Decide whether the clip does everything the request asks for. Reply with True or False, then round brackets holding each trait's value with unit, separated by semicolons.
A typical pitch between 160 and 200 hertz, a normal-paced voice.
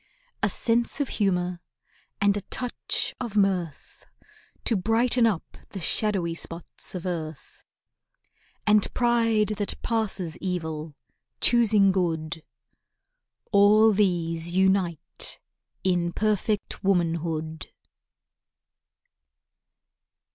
False (190 Hz; 85 wpm)